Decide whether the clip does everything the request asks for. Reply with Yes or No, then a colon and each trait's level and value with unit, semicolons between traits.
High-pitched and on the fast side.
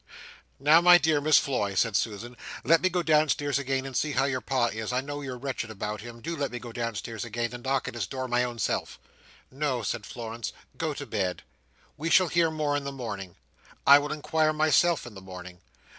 No: low, 130 Hz; fast, 220 wpm